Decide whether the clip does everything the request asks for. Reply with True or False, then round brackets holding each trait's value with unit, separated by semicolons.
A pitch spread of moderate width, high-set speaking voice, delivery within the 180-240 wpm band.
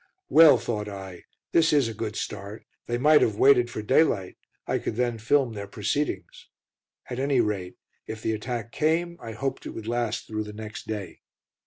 False (4.0 semitones; 115 Hz; 185 wpm)